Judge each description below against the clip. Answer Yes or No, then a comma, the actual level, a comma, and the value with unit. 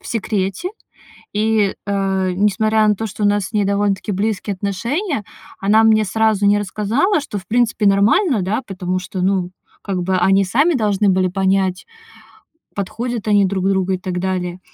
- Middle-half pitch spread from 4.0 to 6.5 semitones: No, narrow, 2.4 semitones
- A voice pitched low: No, high, 200 Hz